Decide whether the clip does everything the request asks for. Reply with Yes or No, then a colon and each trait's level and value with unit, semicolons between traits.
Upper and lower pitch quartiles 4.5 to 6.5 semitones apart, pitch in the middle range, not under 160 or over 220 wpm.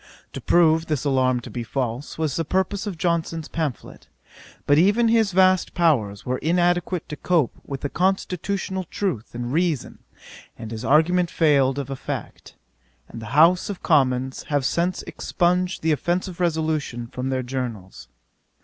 No: wide, 5.4 semitones; medium, 160 Hz; average, 150 wpm